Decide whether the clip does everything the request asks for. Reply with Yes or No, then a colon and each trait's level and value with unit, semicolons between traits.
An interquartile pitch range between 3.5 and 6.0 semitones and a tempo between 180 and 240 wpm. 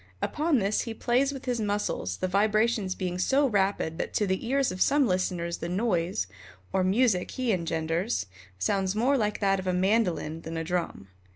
Yes: average, 4.6 semitones; average, 185 wpm